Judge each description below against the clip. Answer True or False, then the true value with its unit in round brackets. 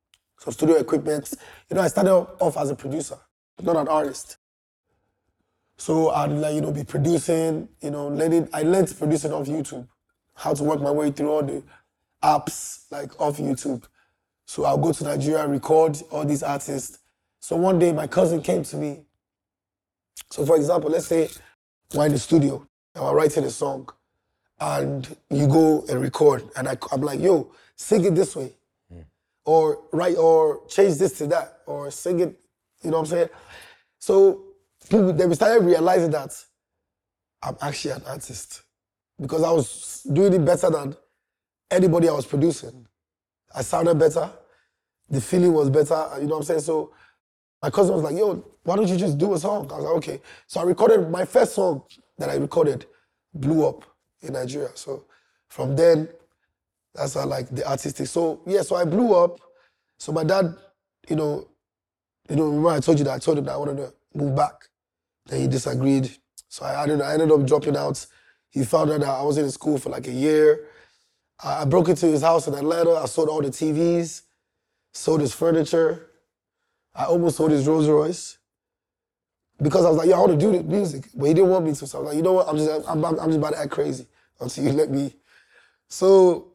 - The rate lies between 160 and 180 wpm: False (195 wpm)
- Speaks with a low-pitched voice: False (155 Hz)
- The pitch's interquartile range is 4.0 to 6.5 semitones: False (3.2 semitones)